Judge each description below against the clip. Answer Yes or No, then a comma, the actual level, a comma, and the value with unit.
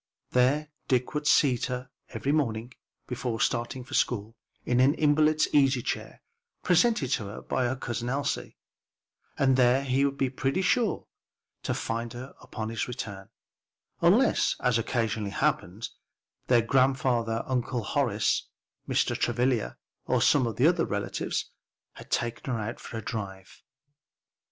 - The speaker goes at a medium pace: Yes, average, 145 wpm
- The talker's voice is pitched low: Yes, low, 125 Hz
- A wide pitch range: No, average, 3.1 semitones